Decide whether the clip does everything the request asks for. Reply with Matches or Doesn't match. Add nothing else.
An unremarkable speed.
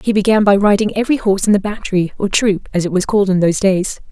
Doesn't match